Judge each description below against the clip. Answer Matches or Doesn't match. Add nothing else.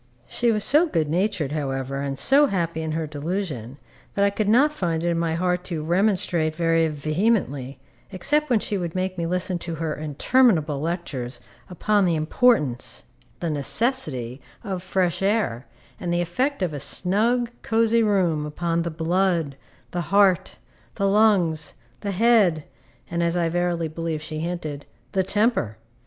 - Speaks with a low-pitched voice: Doesn't match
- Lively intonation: Doesn't match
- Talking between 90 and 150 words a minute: Doesn't match